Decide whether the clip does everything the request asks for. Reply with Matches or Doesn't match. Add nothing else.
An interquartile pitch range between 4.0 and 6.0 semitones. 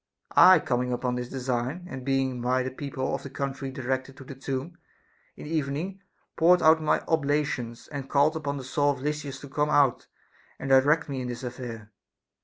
Doesn't match